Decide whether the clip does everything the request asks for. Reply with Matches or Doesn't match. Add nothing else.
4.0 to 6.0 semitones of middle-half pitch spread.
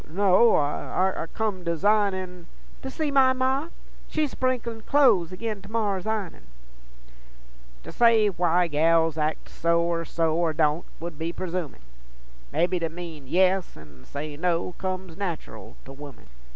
Matches